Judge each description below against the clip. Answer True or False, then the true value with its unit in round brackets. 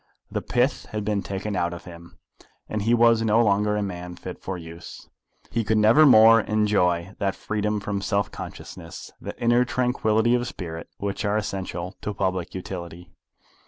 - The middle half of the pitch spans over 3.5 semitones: False (3.2 semitones)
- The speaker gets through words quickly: False (170 wpm)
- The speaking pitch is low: True (100 Hz)